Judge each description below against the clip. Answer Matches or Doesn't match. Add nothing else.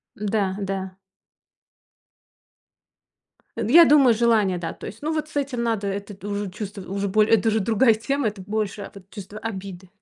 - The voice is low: Doesn't match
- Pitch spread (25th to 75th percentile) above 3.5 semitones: Doesn't match